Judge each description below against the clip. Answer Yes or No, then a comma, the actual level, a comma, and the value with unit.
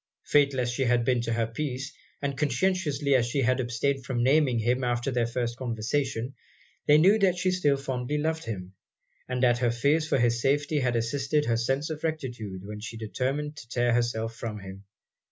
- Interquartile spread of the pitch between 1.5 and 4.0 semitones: Yes, average, 3.6 semitones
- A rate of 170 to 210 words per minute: Yes, average, 195 wpm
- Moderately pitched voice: No, low, 125 Hz